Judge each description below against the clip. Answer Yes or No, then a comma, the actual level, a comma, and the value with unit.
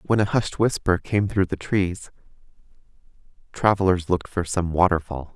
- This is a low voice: Yes, very low, 95 Hz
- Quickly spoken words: No, average, 145 wpm